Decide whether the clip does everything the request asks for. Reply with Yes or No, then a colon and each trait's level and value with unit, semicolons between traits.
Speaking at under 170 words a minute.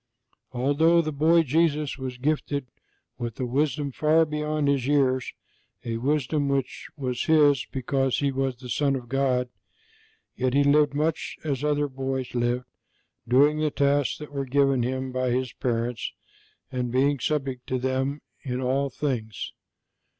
Yes: average, 150 wpm